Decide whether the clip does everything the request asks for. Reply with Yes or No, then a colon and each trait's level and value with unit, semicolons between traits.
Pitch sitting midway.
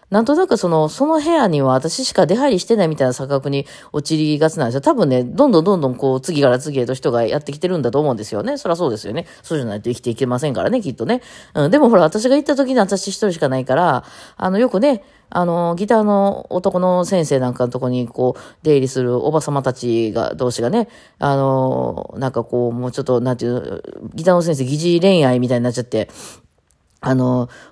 Yes: medium, 145 Hz